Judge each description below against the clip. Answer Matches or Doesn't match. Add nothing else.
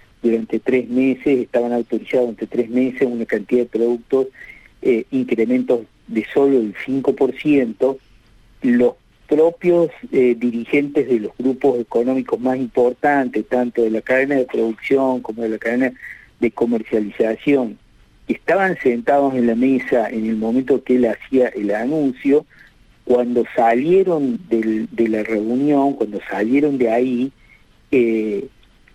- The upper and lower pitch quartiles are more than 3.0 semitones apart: Doesn't match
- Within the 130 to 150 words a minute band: Matches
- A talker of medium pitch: Doesn't match